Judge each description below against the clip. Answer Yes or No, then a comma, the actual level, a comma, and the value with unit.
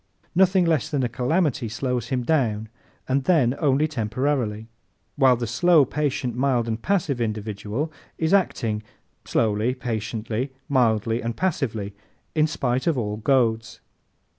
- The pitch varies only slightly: No, average, 4.7 semitones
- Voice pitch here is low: Yes, low, 125 Hz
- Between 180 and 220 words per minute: No, slow, 135 wpm